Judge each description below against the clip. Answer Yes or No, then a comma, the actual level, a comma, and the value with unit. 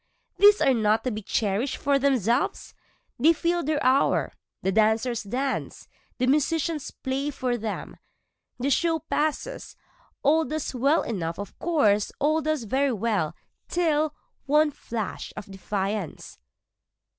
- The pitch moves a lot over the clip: Yes, wide, 5.8 semitones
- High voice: Yes, very high, 265 Hz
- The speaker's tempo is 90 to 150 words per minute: Yes, slow, 135 wpm